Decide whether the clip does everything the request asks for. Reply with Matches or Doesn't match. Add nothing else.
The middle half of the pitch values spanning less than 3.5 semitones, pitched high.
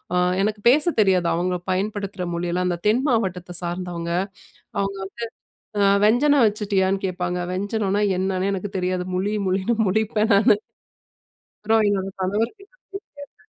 Matches